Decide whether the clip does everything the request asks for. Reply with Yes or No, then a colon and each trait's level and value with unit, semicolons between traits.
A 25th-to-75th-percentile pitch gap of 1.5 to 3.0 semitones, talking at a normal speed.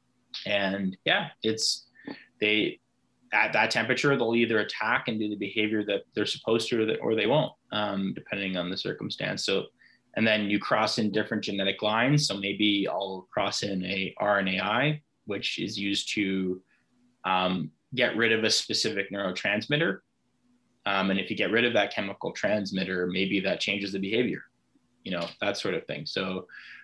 Yes: narrow, 2.4 semitones; average, 170 wpm